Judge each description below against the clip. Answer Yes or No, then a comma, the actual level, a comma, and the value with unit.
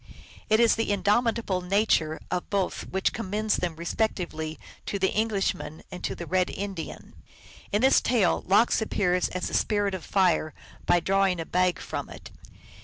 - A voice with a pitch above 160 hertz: Yes, high, 190 Hz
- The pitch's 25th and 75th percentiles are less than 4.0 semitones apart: Yes, average, 3.0 semitones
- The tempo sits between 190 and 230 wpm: No, average, 165 wpm